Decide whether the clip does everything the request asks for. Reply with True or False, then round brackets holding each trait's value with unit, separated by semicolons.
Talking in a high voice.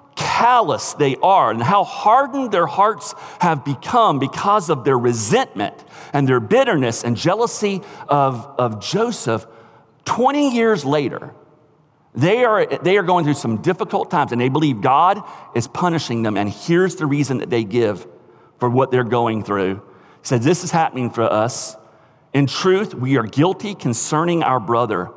False (140 Hz)